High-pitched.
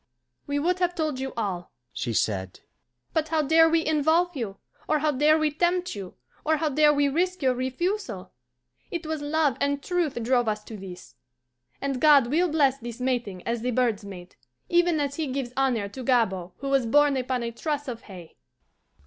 Yes: very high, 275 Hz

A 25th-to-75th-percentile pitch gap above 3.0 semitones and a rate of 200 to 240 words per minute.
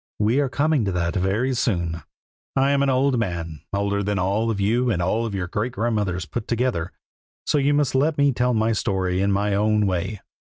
Yes: average, 4.8 semitones; fast, 205 wpm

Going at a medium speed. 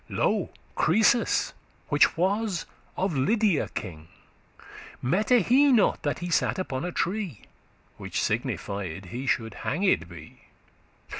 No: slow, 125 wpm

